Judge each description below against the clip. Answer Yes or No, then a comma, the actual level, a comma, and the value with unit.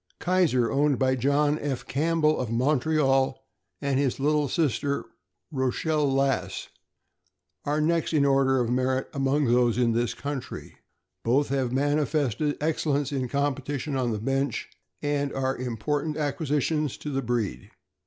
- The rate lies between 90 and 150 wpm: Yes, slow, 135 wpm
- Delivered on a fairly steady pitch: Yes, narrow, 2.3 semitones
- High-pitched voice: No, medium, 140 Hz